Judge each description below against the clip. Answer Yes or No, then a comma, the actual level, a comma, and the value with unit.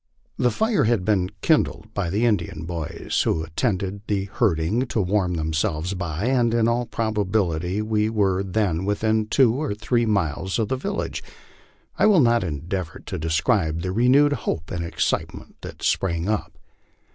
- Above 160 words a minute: Yes, average, 170 wpm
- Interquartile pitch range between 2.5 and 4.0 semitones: No, average, 5.0 semitones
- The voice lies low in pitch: Yes, low, 100 Hz